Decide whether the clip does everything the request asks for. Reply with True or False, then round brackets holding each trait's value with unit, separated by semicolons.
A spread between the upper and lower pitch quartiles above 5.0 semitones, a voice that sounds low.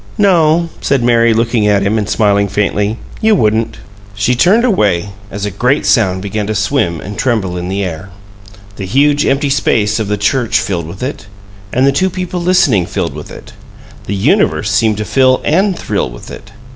True (5.4 semitones; 110 Hz)